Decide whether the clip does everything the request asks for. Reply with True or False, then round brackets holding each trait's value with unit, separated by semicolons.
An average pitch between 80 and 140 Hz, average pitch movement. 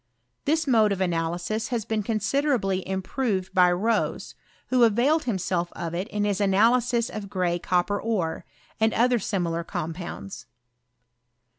False (205 Hz; 4.3 semitones)